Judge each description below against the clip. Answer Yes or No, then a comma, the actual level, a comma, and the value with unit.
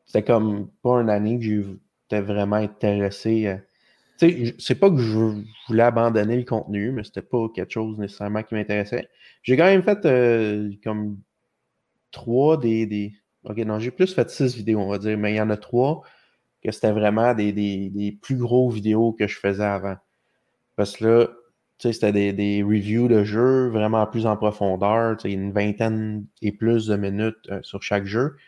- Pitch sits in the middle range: No, low, 110 Hz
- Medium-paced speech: Yes, average, 190 wpm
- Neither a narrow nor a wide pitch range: No, narrow, 2.3 semitones